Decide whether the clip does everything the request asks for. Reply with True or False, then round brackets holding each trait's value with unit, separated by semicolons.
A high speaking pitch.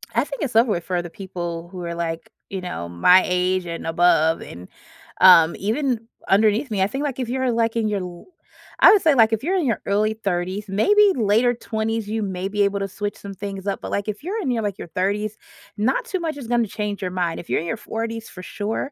True (205 Hz)